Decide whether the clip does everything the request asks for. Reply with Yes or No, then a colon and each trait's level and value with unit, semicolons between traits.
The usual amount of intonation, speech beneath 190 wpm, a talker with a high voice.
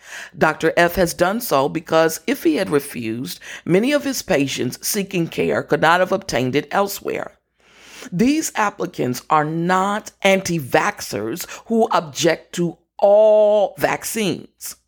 No: average, 4.9 semitones; slow, 135 wpm; medium, 175 Hz